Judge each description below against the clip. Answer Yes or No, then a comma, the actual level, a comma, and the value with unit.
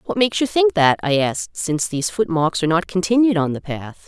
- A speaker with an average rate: No, fast, 235 wpm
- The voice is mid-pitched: Yes, medium, 170 Hz